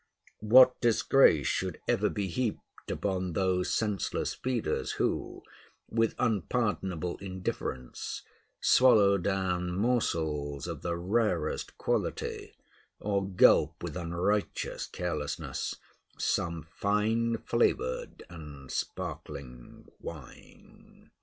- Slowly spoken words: Yes, slow, 90 wpm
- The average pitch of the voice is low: Yes, very low, 95 Hz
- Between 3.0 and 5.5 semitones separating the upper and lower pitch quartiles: Yes, average, 4.5 semitones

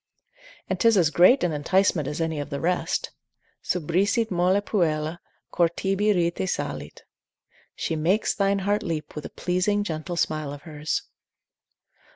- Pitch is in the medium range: Yes, medium, 175 Hz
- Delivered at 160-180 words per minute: No, average, 150 wpm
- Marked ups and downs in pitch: No, average, 3.9 semitones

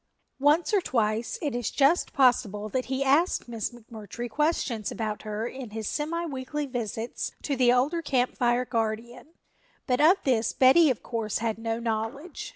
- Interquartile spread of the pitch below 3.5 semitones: No, average, 4.0 semitones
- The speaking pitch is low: No, high, 245 Hz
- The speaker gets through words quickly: No, average, 165 wpm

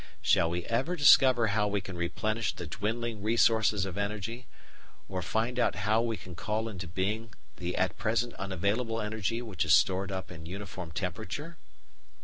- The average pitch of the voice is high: No, low, 105 Hz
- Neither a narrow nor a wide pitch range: Yes, average, 3.5 semitones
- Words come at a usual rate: Yes, average, 165 wpm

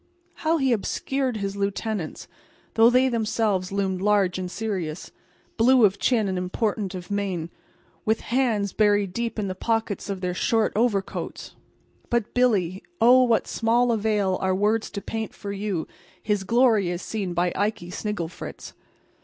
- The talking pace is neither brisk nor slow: Yes, average, 150 wpm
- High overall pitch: Yes, high, 210 Hz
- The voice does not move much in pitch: No, average, 3.2 semitones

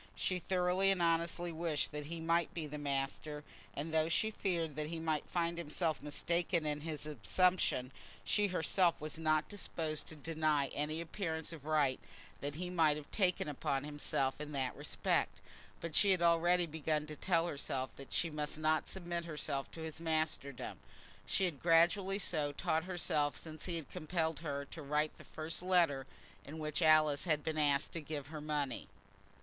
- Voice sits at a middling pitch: Yes, medium, 155 Hz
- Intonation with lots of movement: No, narrow, 2.4 semitones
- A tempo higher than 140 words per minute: Yes, average, 175 wpm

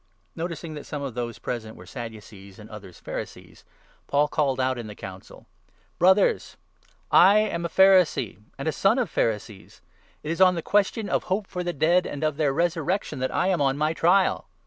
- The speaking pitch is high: No, medium, 155 Hz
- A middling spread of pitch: No, wide, 7.1 semitones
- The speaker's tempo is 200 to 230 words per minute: Yes, fast, 205 wpm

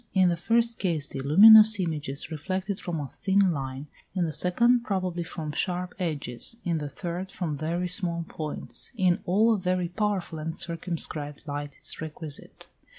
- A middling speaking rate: Yes, average, 170 wpm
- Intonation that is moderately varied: Yes, average, 3.6 semitones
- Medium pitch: Yes, medium, 175 Hz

